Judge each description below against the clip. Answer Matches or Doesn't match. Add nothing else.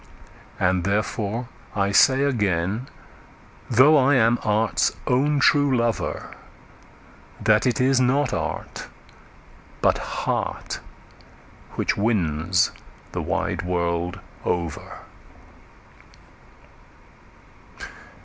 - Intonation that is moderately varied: Doesn't match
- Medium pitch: Doesn't match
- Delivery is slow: Matches